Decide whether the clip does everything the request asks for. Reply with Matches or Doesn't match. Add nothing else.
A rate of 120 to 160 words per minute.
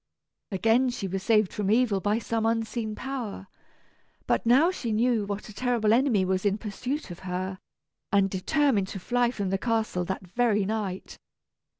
Doesn't match